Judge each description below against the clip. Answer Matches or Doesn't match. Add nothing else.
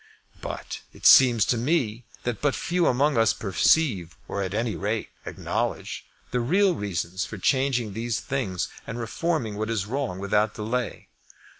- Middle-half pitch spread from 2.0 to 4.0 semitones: Doesn't match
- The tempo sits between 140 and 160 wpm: Matches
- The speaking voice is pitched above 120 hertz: Doesn't match